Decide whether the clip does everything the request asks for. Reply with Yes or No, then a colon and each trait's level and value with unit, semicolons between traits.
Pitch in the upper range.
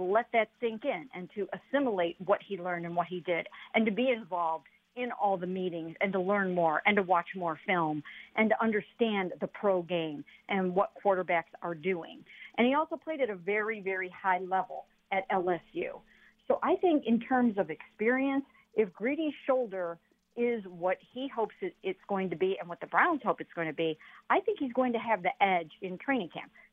Yes: high, 195 Hz